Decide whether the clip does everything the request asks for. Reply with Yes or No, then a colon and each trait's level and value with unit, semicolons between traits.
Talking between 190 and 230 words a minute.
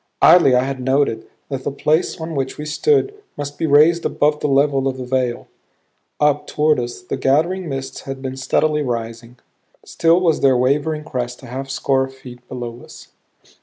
No: average, 180 wpm